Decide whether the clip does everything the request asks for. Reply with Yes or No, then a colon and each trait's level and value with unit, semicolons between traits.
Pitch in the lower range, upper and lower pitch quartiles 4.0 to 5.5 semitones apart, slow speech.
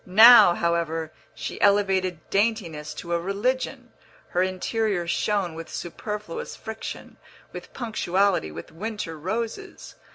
No: high, 190 Hz; average, 4.4 semitones; slow, 110 wpm